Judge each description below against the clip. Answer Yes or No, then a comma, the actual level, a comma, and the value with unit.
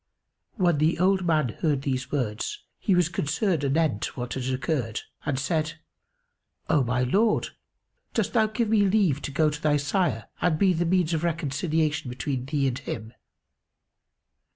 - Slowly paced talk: No, average, 160 wpm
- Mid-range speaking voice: Yes, medium, 155 Hz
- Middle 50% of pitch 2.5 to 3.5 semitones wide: No, average, 4.8 semitones